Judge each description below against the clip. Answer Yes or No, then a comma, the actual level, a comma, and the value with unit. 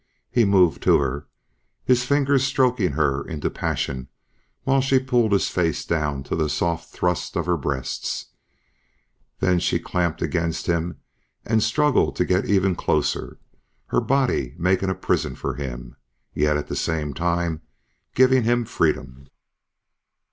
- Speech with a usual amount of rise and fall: No, wide, 7.9 semitones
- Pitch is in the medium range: No, very low, 85 Hz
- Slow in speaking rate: No, average, 150 wpm